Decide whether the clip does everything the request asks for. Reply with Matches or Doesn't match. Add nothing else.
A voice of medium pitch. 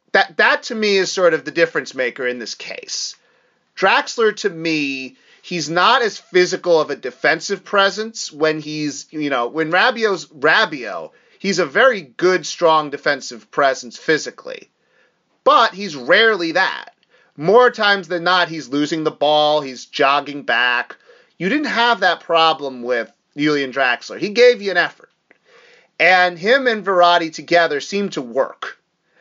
Matches